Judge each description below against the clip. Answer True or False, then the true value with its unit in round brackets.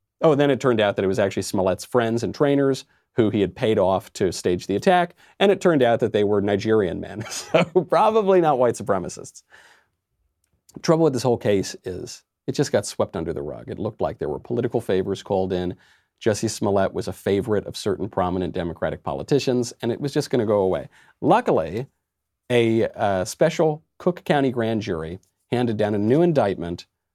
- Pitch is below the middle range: True (115 Hz)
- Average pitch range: False (6.9 semitones)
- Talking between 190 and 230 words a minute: True (200 wpm)